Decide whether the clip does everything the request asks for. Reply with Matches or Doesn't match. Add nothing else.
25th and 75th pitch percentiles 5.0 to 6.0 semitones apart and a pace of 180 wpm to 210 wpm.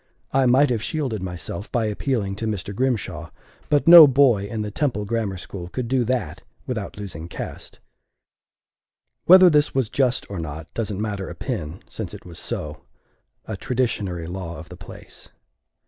Doesn't match